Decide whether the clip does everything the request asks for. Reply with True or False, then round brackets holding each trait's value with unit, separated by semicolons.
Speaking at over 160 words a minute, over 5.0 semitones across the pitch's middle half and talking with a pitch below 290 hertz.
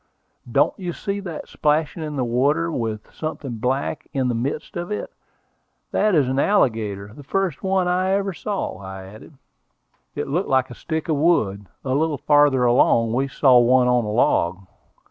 True (180 wpm; 5.6 semitones; 140 Hz)